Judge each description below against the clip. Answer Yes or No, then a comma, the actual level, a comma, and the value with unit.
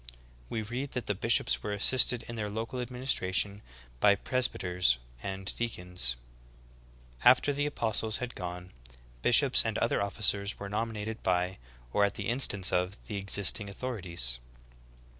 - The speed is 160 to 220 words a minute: No, average, 150 wpm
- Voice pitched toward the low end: Yes, low, 105 Hz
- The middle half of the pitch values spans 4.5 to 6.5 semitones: No, average, 3.9 semitones